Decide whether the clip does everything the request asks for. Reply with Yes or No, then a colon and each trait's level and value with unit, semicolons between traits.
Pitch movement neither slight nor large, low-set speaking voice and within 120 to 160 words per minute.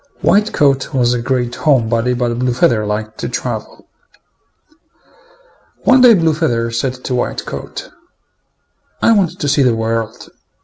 Yes: average, 4.2 semitones; low, 125 Hz; average, 150 wpm